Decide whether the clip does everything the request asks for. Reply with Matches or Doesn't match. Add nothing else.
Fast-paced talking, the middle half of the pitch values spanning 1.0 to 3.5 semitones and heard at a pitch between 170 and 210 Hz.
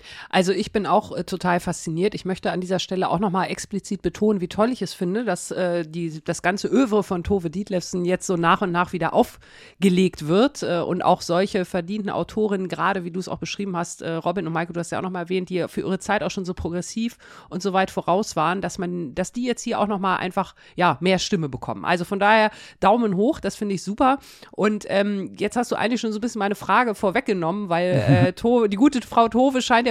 Matches